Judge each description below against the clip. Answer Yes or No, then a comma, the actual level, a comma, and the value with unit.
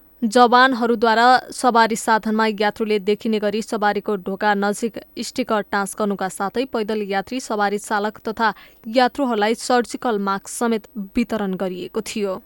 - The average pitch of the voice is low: No, high, 220 Hz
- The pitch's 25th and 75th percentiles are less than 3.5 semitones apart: Yes, narrow, 2.6 semitones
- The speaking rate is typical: No, slow, 115 wpm